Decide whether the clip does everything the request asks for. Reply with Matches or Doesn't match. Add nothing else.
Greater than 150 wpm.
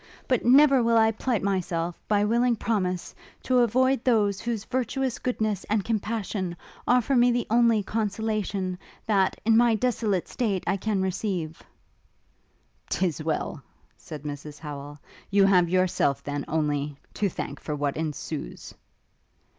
Doesn't match